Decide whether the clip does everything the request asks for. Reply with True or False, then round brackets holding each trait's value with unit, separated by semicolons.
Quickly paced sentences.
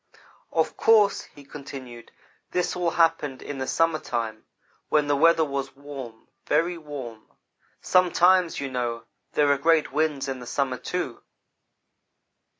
False (145 wpm)